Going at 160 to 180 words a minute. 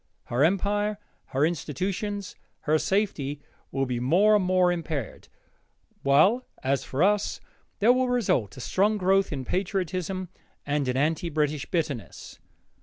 No: slow, 135 wpm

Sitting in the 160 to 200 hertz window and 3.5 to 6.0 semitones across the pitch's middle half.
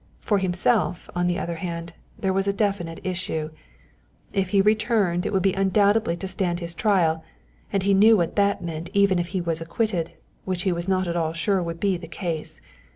No: medium, 185 Hz; average, 2.7 semitones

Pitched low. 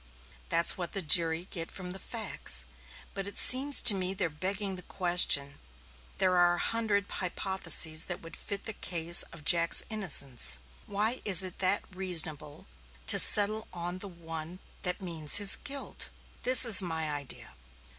No: medium, 180 Hz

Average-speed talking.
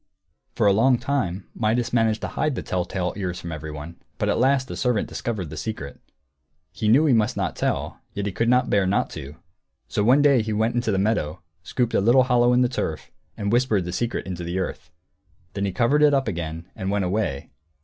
No: fast, 220 wpm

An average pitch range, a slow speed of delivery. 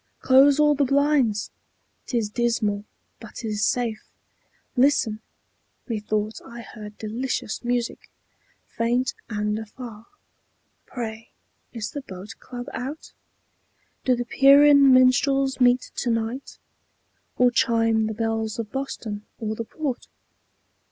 Yes: average, 3.2 semitones; slow, 120 wpm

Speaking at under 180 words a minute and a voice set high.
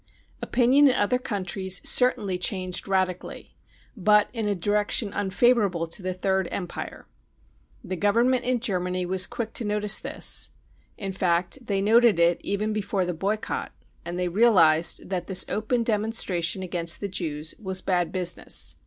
Yes: average, 150 wpm; high, 195 Hz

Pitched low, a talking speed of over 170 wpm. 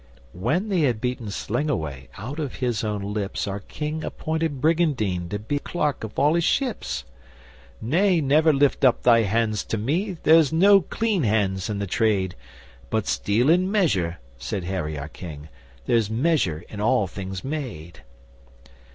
No: low, 115 Hz; average, 160 wpm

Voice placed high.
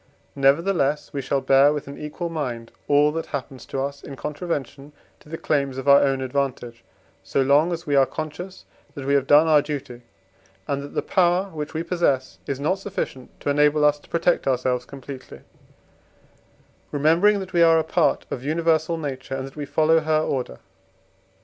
No: medium, 145 Hz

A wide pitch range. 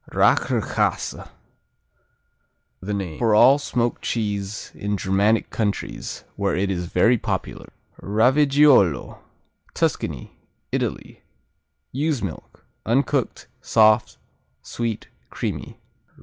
No: average, 4.0 semitones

